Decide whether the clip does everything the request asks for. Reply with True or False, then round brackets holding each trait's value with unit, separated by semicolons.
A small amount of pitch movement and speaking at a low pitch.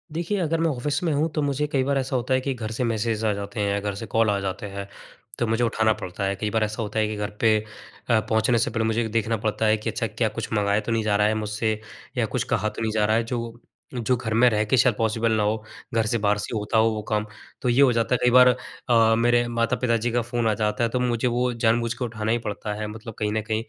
True (2.0 semitones; 115 Hz)